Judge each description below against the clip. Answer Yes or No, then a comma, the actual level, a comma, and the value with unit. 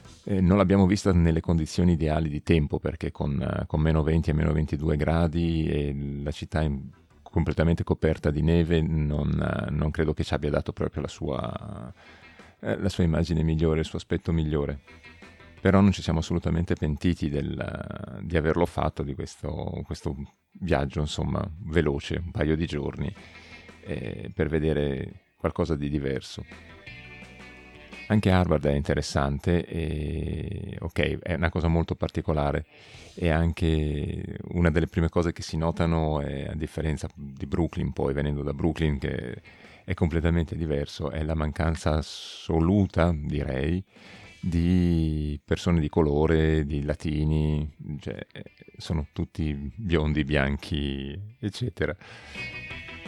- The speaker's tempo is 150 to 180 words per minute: No, average, 135 wpm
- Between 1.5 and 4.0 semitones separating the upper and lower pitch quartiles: Yes, narrow, 2.6 semitones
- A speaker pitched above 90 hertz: No, very low, 80 Hz